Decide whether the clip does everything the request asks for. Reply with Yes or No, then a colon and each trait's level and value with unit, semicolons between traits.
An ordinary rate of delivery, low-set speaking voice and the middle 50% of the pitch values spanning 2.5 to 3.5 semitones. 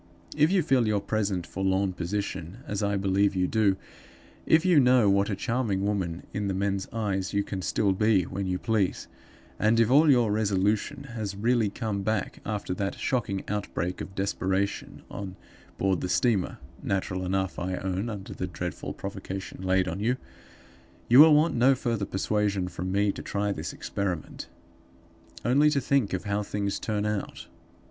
Yes: average, 170 wpm; low, 100 Hz; average, 2.8 semitones